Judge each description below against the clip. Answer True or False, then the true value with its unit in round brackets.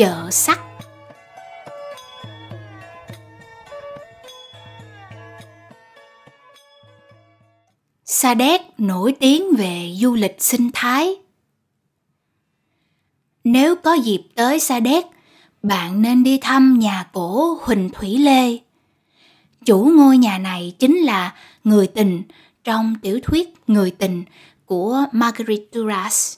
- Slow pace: True (95 wpm)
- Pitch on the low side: False (205 Hz)